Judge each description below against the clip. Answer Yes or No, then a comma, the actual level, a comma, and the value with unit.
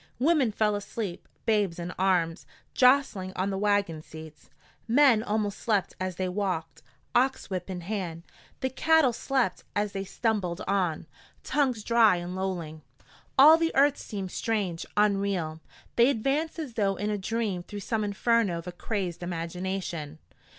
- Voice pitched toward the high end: Yes, high, 200 Hz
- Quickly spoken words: No, average, 150 wpm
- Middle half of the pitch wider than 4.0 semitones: Yes, average, 4.4 semitones